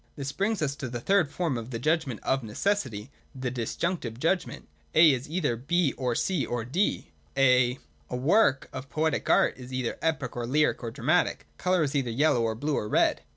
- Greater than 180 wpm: Yes, average, 200 wpm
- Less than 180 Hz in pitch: Yes, low, 135 Hz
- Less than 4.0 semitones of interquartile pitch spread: No, average, 4.8 semitones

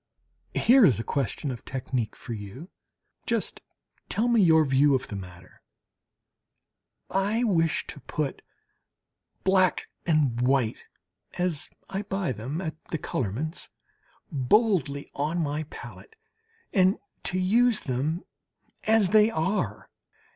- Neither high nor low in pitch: Yes, medium, 155 Hz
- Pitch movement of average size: No, wide, 6.6 semitones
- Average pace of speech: No, slow, 120 wpm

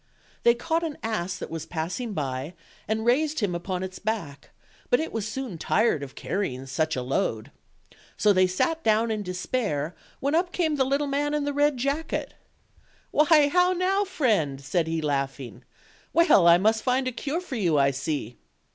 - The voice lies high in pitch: Yes, high, 220 Hz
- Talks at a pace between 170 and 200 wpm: Yes, average, 180 wpm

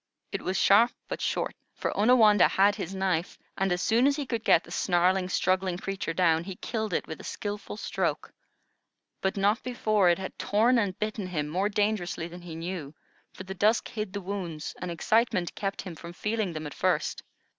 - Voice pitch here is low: No, high, 190 Hz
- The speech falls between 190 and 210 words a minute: Yes, average, 200 wpm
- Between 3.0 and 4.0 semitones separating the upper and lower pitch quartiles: Yes, average, 3.3 semitones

